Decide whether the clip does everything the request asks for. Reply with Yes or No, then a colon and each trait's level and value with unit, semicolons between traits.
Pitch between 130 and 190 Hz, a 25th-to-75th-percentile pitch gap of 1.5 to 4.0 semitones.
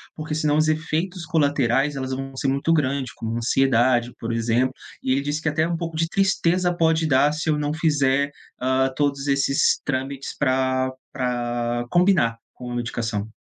Yes: medium, 140 Hz; average, 3.4 semitones